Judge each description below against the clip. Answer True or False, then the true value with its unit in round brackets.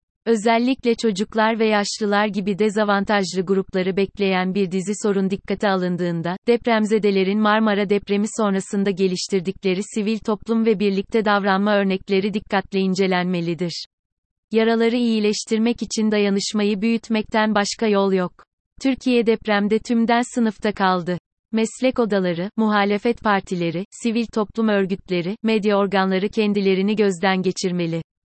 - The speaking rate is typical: True (110 wpm)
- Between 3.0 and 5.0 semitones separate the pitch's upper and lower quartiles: False (2.5 semitones)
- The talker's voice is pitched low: False (205 Hz)